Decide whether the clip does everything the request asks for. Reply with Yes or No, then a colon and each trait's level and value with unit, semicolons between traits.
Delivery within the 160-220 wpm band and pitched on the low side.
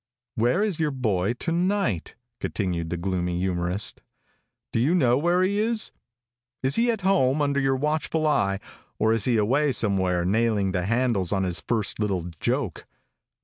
Yes: average, 165 wpm; low, 115 Hz